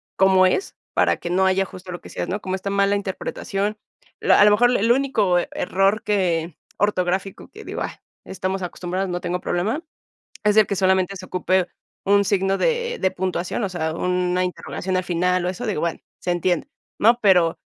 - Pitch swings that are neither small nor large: No, narrow, 2.0 semitones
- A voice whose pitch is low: No, high, 190 Hz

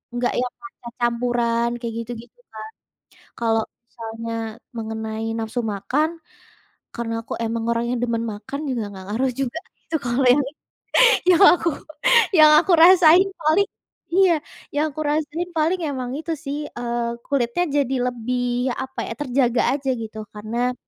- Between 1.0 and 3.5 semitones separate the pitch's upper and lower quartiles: No, average, 4.3 semitones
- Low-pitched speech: No, high, 245 Hz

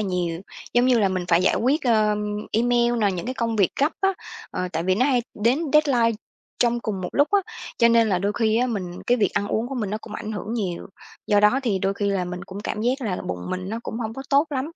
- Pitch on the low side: No, high, 220 Hz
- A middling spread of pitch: Yes, average, 3.9 semitones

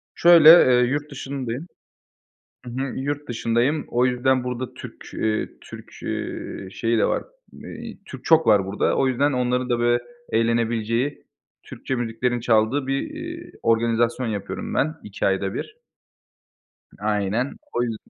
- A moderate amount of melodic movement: Yes, average, 3.2 semitones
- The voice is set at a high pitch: No, low, 125 Hz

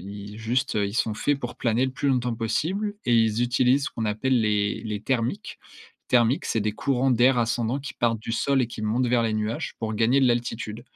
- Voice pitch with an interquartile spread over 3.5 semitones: No, average, 2.8 semitones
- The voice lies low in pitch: Yes, low, 120 Hz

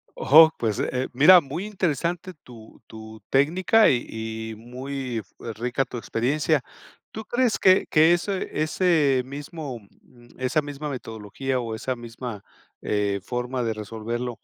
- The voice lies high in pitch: No, low, 130 Hz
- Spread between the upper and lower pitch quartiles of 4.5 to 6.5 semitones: Yes, average, 5.3 semitones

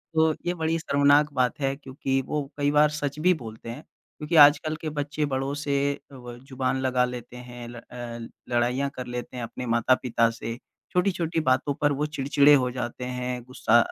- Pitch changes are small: No, average, 3.2 semitones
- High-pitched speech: No, low, 135 Hz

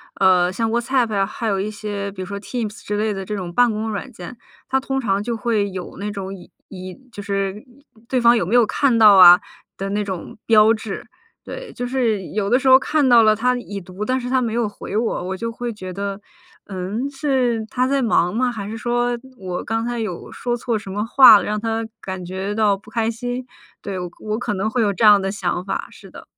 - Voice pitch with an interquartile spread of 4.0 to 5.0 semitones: No, average, 3.4 semitones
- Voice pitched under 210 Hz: No, high, 215 Hz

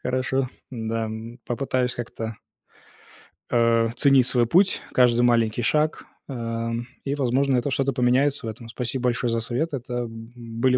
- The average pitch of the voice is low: Yes, low, 120 Hz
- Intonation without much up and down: Yes, narrow, 2.2 semitones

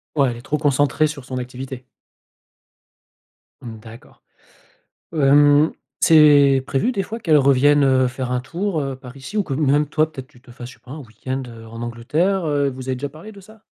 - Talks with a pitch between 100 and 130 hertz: No, medium, 140 Hz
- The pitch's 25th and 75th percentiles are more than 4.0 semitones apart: No, average, 3.2 semitones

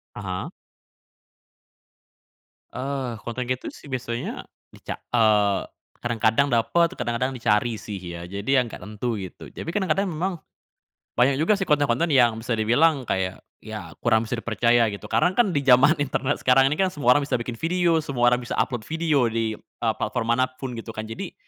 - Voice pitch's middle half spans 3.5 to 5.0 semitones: Yes, average, 4.2 semitones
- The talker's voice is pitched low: Yes, low, 125 Hz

